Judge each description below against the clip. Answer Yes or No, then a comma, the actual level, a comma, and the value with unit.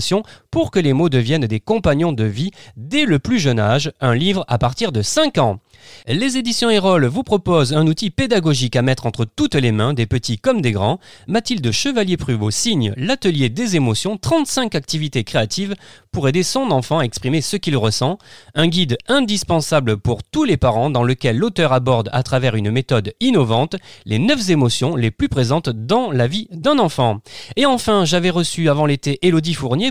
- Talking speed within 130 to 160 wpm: No, average, 185 wpm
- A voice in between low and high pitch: Yes, medium, 145 Hz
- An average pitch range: No, wide, 7.1 semitones